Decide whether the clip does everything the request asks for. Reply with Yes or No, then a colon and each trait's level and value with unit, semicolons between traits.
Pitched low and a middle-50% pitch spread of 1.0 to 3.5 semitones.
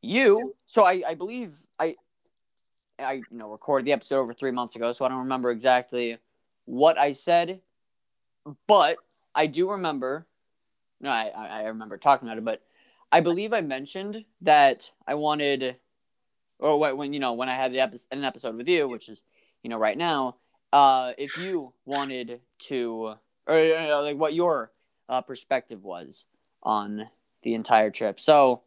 No: low, 130 Hz; average, 4.2 semitones